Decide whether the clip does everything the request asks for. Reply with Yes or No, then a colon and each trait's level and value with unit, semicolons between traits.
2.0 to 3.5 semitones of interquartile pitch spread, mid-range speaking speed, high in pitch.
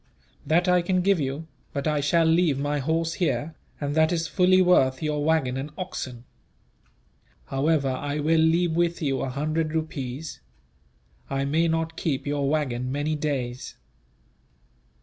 No: average, 2.9 semitones; average, 150 wpm; medium, 155 Hz